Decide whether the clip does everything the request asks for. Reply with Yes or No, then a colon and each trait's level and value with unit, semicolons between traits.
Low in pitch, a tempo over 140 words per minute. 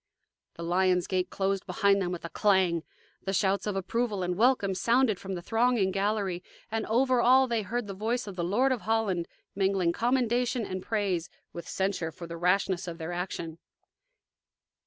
No: high, 195 Hz; average, 180 wpm